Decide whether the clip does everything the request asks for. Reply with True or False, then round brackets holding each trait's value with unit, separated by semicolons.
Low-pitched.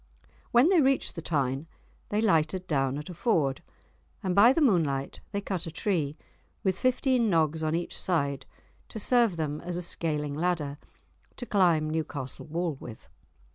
False (165 Hz)